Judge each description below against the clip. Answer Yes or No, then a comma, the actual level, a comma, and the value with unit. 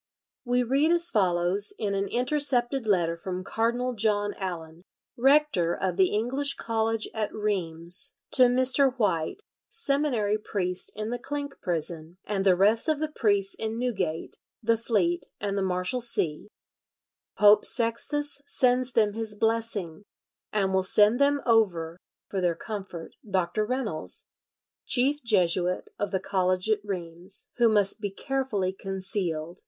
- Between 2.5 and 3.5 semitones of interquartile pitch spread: No, average, 4.9 semitones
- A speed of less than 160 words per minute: Yes, average, 140 wpm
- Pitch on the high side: Yes, high, 210 Hz